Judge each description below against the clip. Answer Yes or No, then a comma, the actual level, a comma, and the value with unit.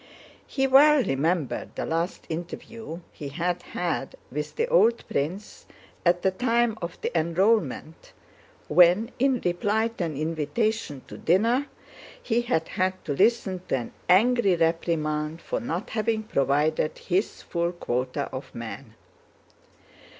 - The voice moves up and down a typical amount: No, wide, 6.1 semitones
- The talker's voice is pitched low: No, medium, 175 Hz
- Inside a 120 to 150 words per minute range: Yes, slow, 135 wpm